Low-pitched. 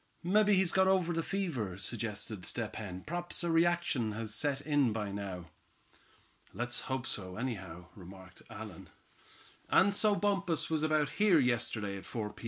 Yes: low, 125 Hz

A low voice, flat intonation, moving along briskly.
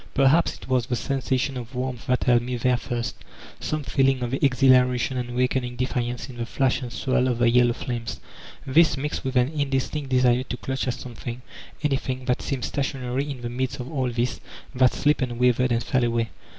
Yes: low, 125 Hz; narrow, 1.6 semitones; fast, 210 wpm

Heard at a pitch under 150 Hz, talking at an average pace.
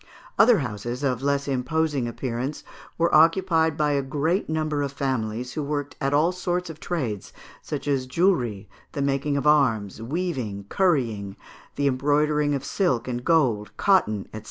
Yes: medium, 140 Hz; average, 155 wpm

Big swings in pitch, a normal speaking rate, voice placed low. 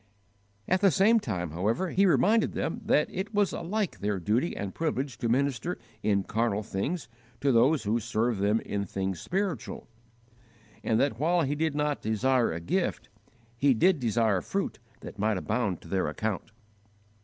Yes: wide, 8.0 semitones; average, 165 wpm; low, 120 Hz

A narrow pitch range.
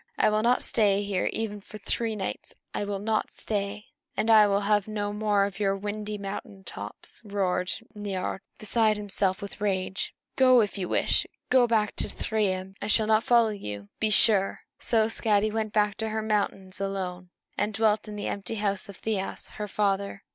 Yes: narrow, 1.6 semitones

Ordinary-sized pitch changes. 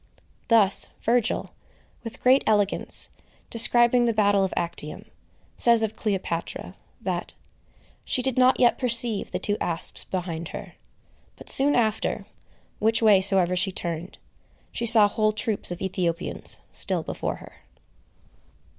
Yes: average, 3.9 semitones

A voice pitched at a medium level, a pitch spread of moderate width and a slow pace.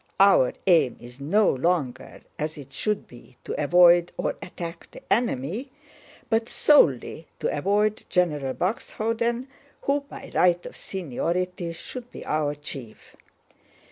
No: medium, 175 Hz; wide, 6.4 semitones; slow, 130 wpm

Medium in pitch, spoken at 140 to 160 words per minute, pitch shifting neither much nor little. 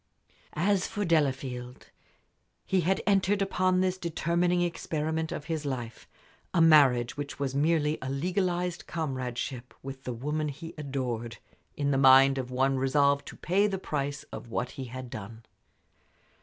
Yes: medium, 145 Hz; average, 150 wpm; average, 4.6 semitones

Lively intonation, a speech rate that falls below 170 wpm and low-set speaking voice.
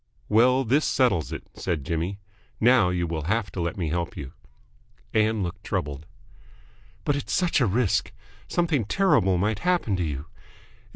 Yes: wide, 6.7 semitones; average, 160 wpm; low, 100 Hz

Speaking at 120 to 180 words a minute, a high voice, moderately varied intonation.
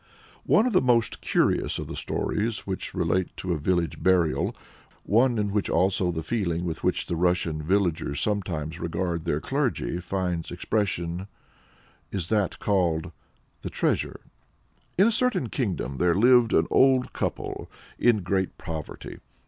No: average, 150 wpm; very low, 95 Hz; average, 4.3 semitones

